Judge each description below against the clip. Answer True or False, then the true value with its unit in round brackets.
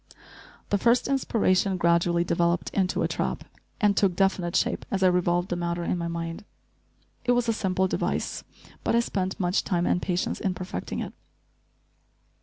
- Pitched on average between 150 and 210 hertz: True (185 Hz)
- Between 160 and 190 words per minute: True (170 wpm)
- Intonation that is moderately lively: False (2.3 semitones)